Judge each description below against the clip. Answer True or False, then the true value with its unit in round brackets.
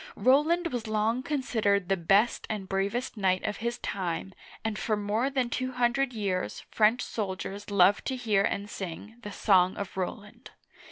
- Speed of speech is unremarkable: True (170 wpm)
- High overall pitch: True (210 Hz)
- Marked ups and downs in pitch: False (3.7 semitones)